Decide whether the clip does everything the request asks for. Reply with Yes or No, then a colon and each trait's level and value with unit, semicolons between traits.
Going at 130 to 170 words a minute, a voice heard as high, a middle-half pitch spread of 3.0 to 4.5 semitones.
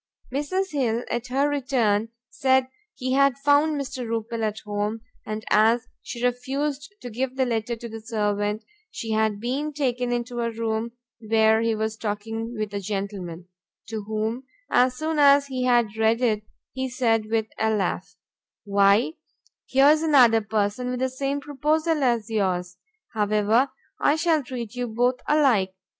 Yes: average, 160 wpm; high, 235 Hz; average, 3.4 semitones